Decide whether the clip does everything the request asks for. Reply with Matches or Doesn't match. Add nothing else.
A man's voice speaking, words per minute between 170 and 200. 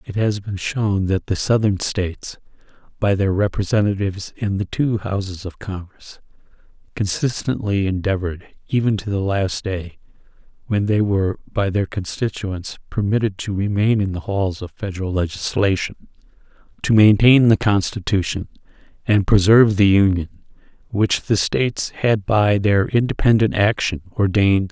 Doesn't match